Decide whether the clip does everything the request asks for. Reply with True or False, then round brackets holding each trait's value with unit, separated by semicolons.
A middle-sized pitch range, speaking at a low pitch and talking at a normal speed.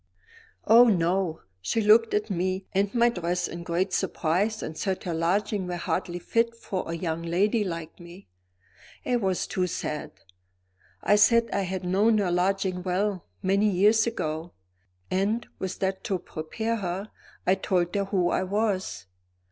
False (3.0 semitones; 190 Hz; 160 wpm)